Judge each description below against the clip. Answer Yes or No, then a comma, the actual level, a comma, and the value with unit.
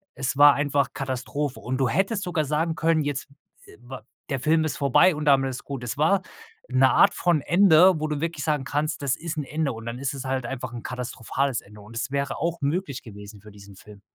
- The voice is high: No, medium, 140 Hz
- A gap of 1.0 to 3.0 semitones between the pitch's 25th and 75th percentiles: No, average, 3.6 semitones